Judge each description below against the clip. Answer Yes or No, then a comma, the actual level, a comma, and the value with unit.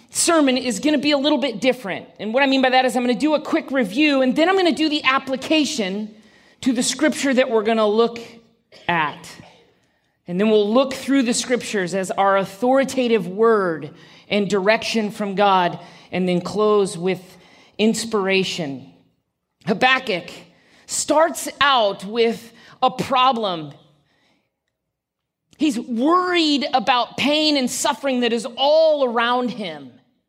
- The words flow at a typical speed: Yes, average, 155 wpm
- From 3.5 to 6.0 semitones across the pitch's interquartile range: Yes, average, 5.1 semitones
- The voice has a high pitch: Yes, high, 240 Hz